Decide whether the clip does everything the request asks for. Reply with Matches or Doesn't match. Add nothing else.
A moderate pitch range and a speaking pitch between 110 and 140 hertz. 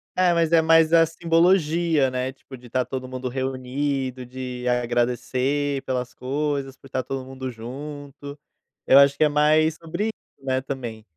Matches